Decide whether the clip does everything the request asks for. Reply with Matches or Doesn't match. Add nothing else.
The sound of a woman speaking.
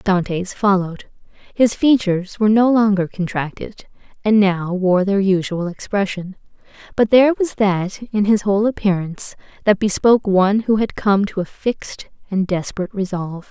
Matches